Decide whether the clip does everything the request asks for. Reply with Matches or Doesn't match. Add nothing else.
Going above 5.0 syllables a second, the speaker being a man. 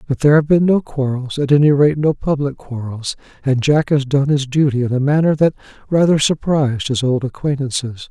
Matches